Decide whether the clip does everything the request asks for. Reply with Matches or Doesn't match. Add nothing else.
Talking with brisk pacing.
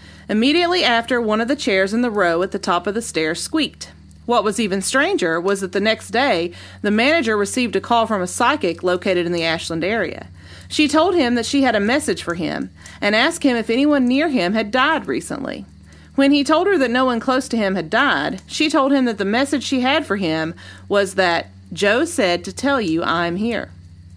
Matches